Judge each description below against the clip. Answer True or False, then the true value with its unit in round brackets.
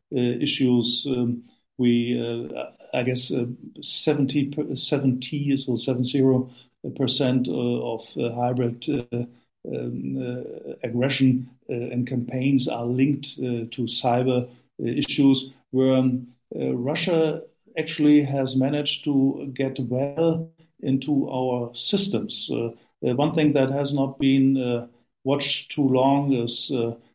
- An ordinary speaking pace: False (125 wpm)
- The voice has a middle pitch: False (130 Hz)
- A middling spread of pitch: False (2.3 semitones)